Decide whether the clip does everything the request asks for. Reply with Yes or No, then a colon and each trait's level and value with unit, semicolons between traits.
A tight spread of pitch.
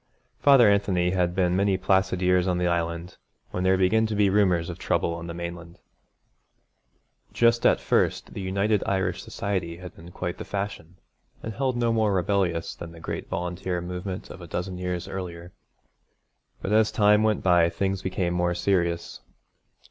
Yes: narrow, 2.3 semitones